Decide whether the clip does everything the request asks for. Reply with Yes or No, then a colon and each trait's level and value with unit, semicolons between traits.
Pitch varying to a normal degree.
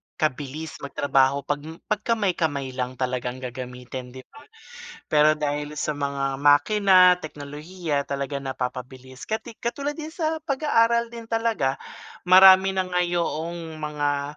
No: wide, 5.7 semitones